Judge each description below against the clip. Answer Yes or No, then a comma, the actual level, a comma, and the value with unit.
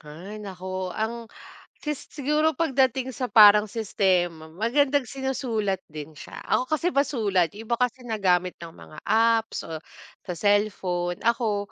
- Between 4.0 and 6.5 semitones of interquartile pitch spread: Yes, wide, 5.5 semitones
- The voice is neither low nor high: No, high, 215 Hz